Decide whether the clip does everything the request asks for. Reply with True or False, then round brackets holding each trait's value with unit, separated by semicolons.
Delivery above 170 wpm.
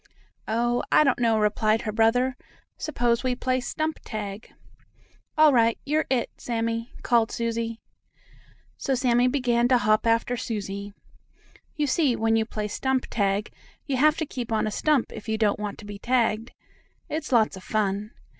False (165 wpm)